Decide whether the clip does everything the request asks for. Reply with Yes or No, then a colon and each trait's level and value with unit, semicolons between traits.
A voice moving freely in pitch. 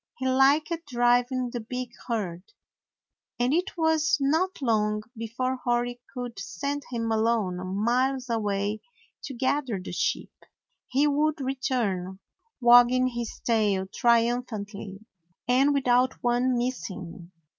No: average, 3.1 semitones